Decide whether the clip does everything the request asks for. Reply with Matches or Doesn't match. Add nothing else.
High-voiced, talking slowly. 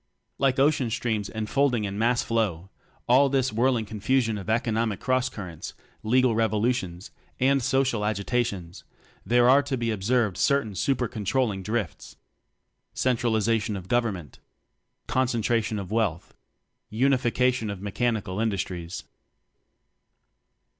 Doesn't match